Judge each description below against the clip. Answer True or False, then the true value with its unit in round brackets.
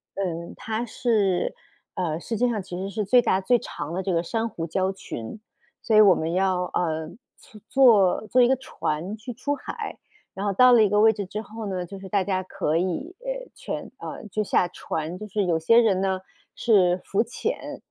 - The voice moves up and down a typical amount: True (3.6 semitones)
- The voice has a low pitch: False (195 Hz)